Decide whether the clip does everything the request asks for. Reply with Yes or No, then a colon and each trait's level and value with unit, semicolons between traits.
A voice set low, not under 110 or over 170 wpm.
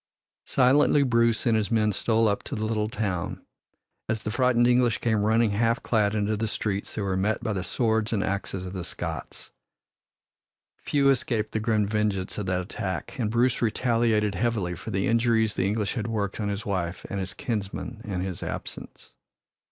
No: low, 110 Hz; average, 185 wpm